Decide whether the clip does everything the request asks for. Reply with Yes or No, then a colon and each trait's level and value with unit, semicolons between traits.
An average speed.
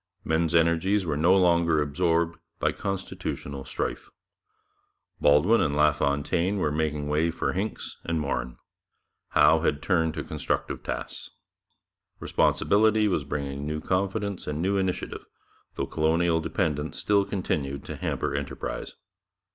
No: slow, 125 wpm